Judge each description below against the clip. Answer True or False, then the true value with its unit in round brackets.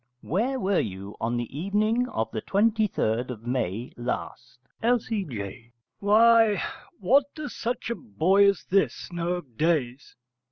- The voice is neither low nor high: True (180 Hz)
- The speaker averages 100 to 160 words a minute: True (135 wpm)